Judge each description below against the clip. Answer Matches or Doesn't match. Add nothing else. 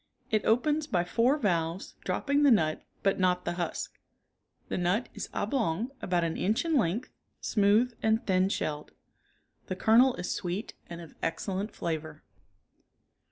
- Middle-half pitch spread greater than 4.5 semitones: Matches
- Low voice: Doesn't match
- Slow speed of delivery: Doesn't match